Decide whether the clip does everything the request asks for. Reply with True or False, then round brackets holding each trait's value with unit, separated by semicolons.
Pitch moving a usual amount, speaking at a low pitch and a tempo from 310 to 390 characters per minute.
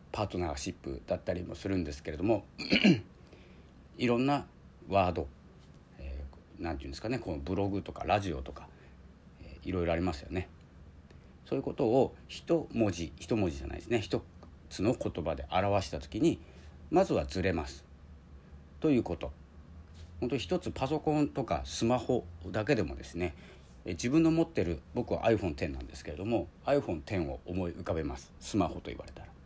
True (5.0 semitones; 85 Hz; 360 characters per minute)